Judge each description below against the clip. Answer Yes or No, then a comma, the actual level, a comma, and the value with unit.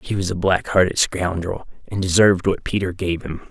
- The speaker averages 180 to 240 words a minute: Yes, fast, 205 wpm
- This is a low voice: Yes, very low, 90 Hz